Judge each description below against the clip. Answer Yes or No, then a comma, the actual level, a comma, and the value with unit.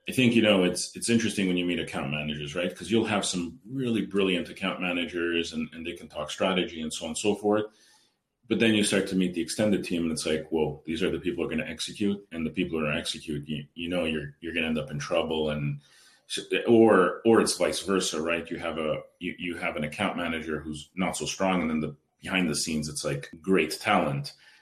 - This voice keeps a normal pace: No, fast, 250 wpm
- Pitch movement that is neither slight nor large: Yes, average, 4.2 semitones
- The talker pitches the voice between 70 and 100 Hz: Yes, very low, 85 Hz